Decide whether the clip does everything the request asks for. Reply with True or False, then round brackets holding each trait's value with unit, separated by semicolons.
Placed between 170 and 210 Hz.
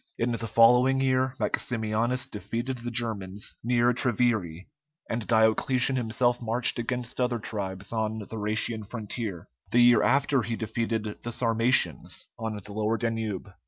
False (115 Hz)